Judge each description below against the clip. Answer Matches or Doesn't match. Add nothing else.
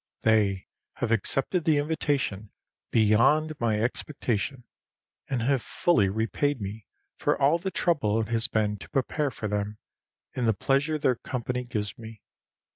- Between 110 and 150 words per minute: Matches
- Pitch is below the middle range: Matches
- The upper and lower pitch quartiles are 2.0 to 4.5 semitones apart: Doesn't match